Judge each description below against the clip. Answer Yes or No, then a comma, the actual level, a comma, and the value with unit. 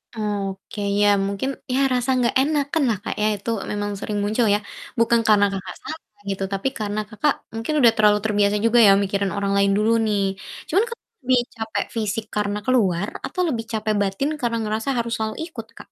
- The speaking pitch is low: No, high, 215 Hz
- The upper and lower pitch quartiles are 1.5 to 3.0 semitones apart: Yes, average, 2.7 semitones